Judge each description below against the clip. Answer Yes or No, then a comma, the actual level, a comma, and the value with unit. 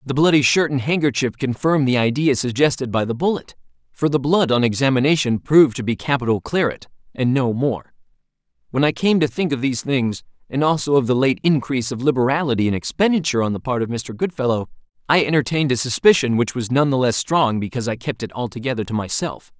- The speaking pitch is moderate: No, low, 130 Hz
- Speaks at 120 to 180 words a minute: No, average, 200 wpm